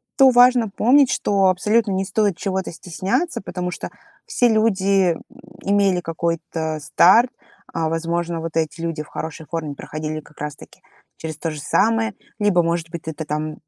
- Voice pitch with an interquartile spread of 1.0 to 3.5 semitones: No, average, 4.2 semitones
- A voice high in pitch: No, medium, 175 Hz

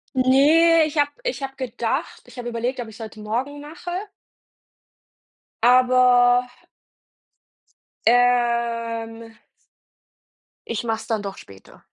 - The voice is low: No, high, 245 Hz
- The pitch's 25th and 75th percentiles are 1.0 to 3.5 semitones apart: Yes, average, 2.8 semitones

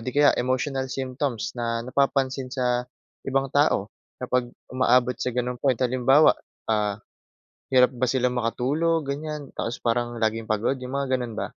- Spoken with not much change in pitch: Yes, narrow, 2.0 semitones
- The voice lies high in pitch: No, low, 125 Hz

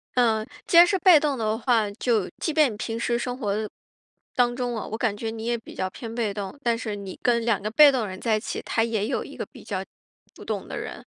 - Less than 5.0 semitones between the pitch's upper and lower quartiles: Yes, narrow, 2.4 semitones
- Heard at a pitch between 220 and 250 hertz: Yes, high, 230 Hz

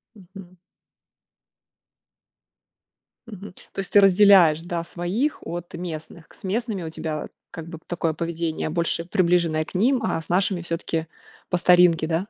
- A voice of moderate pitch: Yes, medium, 175 Hz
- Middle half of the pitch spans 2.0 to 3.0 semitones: Yes, narrow, 2.6 semitones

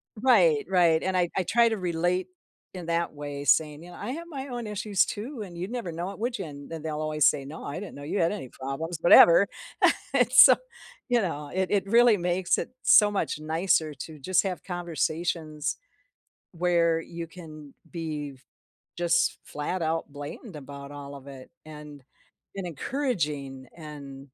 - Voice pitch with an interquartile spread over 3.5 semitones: Yes, average, 4.0 semitones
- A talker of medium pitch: Yes, medium, 170 Hz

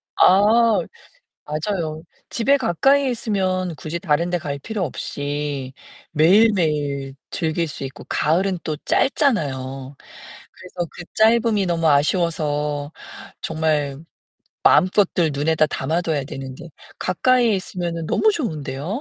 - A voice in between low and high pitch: Yes, medium, 170 Hz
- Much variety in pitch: No, average, 5.0 semitones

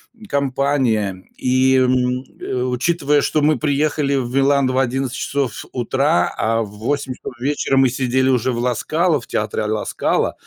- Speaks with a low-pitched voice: Yes, low, 130 Hz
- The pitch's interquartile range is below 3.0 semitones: Yes, narrow, 2.4 semitones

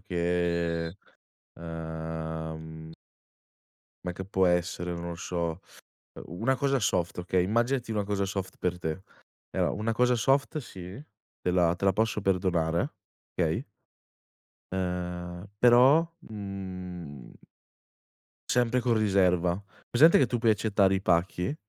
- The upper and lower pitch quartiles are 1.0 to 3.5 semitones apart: No, average, 4.0 semitones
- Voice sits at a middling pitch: No, very low, 90 Hz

